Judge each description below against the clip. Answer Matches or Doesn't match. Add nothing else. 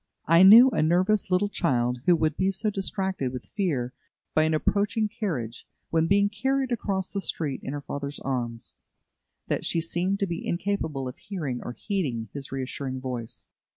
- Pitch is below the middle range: Doesn't match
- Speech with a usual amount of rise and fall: Doesn't match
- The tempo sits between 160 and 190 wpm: Matches